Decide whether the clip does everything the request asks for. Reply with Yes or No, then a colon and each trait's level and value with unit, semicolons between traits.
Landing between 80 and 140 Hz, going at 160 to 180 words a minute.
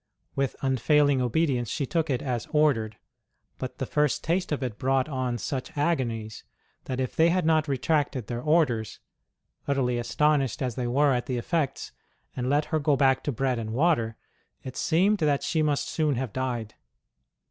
Yes: low, 135 Hz; average, 175 wpm